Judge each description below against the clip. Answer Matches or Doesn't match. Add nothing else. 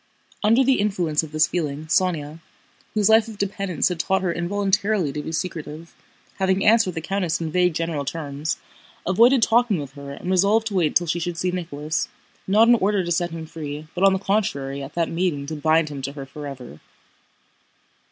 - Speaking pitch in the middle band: Matches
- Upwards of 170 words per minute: Matches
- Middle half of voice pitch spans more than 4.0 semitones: Matches